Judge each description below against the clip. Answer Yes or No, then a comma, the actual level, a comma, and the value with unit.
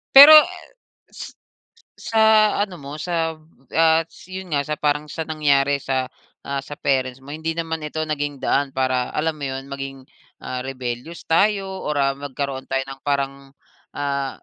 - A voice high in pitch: No, medium, 145 Hz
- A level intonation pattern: No, average, 3.1 semitones